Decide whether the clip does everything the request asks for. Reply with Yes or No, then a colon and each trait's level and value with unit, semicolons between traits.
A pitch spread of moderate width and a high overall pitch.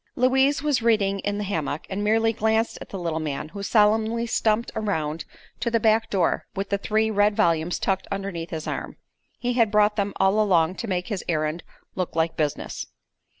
Yes: average, 4.3 semitones; high, 205 Hz